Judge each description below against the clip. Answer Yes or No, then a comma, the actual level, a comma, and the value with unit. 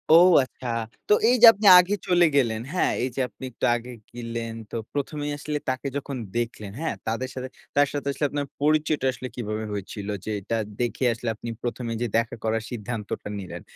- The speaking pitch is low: Yes, low, 125 Hz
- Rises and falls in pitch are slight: No, average, 4.0 semitones